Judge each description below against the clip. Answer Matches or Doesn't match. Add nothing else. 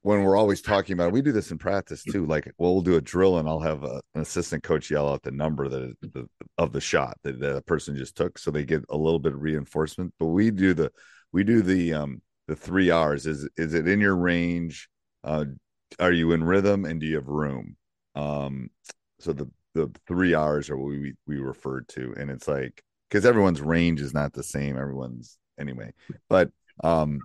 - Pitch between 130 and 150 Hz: Doesn't match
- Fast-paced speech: Matches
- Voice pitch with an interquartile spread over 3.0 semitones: Matches